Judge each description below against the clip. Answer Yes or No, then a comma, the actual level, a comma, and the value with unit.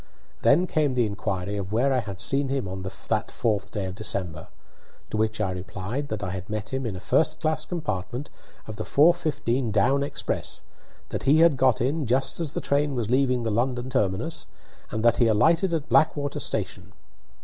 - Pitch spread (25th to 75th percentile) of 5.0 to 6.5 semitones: Yes, wide, 5.5 semitones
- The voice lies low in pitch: Yes, low, 120 Hz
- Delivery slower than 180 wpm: No, average, 185 wpm